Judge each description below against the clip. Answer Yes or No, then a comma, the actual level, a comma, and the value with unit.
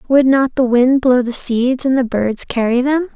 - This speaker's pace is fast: Yes, fast, 230 wpm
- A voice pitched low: No, very high, 255 Hz